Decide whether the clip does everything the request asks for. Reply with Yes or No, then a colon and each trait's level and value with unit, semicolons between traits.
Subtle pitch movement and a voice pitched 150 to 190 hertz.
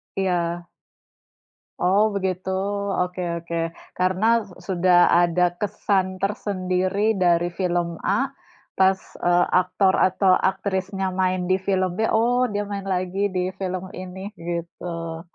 Yes: narrow, 1.7 semitones; medium, 185 Hz